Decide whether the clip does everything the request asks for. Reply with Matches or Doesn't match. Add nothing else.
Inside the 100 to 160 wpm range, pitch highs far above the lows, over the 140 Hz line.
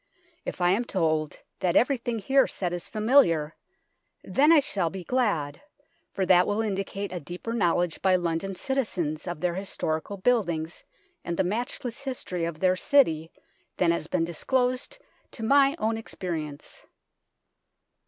Matches